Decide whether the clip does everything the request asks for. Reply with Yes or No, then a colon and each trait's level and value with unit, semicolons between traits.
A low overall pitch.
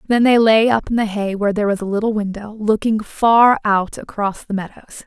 No: high, 215 Hz